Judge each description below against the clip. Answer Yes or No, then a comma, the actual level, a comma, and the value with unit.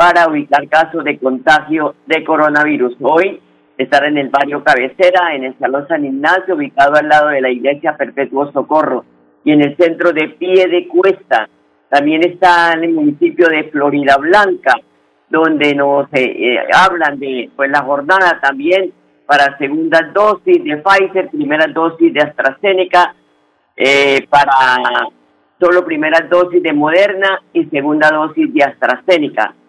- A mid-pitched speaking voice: Yes, medium, 150 Hz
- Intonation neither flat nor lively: Yes, average, 4.0 semitones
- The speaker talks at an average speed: Yes, average, 145 wpm